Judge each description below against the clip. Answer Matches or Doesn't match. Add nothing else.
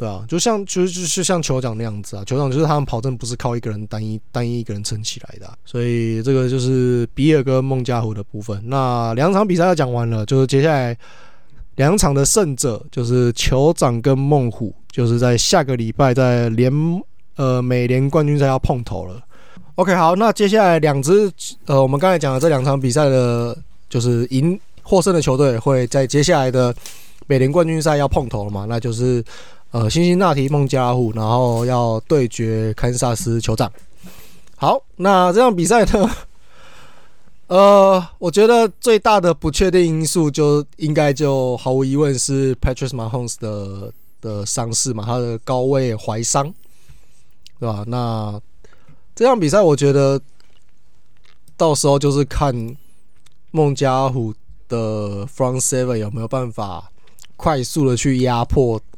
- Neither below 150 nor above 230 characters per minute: Doesn't match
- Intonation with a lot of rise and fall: Doesn't match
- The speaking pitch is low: Matches